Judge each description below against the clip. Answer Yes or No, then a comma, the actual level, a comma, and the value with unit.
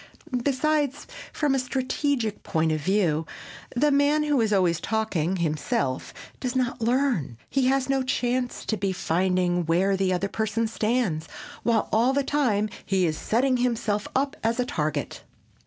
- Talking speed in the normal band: Yes, average, 155 wpm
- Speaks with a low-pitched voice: No, high, 225 Hz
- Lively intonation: Yes, wide, 6.0 semitones